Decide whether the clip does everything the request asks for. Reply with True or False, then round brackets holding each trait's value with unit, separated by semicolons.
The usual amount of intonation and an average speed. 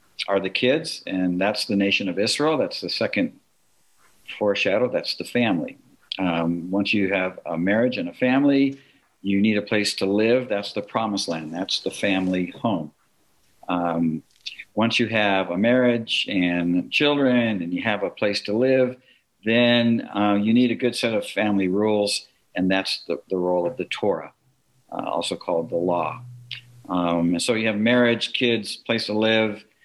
True (4.2 semitones; 175 wpm)